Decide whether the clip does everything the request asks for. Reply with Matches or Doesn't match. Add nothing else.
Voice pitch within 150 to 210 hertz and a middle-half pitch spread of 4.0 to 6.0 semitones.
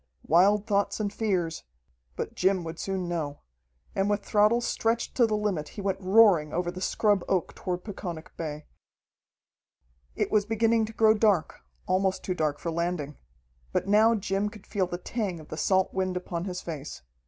Doesn't match